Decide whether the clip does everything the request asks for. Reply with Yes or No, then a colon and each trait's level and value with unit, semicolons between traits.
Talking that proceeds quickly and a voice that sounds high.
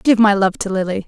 Yes: fast, 280 wpm; high, 200 Hz